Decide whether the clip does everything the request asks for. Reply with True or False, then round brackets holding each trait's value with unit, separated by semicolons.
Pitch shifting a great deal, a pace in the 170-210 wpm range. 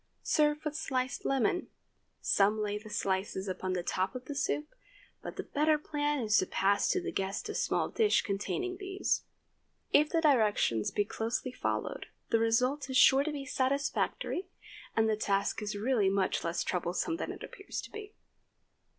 True (6.7 semitones; 175 wpm)